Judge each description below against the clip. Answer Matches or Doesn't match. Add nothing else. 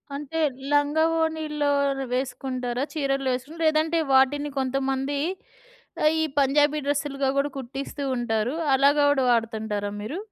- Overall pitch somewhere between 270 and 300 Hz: Matches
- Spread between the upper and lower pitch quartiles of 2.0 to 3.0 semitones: Matches